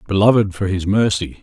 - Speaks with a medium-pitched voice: No, low, 100 Hz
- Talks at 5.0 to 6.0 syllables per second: Yes, 5.5 syllables/s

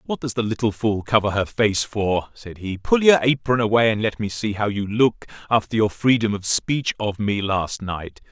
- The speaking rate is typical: No, fast, 225 wpm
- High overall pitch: No, low, 110 Hz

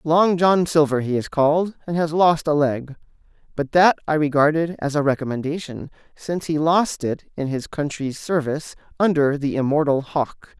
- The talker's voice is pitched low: No, medium, 150 Hz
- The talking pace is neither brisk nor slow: Yes, average, 170 wpm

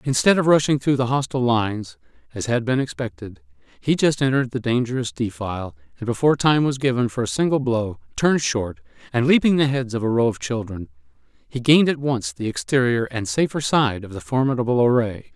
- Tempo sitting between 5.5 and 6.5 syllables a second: Yes, 5.8 syllables/s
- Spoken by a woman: No, male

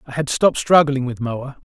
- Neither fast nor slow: No, fast, 210 wpm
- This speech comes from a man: Yes, male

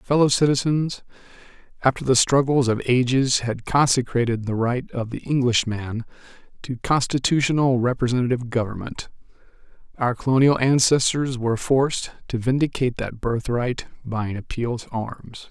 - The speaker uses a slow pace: Yes, slow, 125 wpm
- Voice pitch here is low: Yes, low, 125 Hz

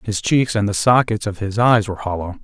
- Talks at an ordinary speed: No, fast, 245 wpm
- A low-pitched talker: Yes, low, 105 Hz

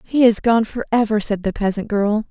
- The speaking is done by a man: No, female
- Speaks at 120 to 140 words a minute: No, fast, 210 wpm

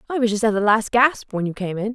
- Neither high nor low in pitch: No, high, 220 Hz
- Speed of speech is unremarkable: No, fast, 340 wpm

